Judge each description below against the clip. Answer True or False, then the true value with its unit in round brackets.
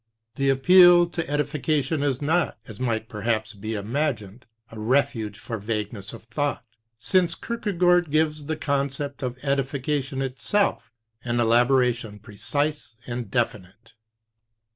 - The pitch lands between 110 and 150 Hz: True (135 Hz)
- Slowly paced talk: True (125 wpm)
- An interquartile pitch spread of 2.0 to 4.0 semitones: False (4.8 semitones)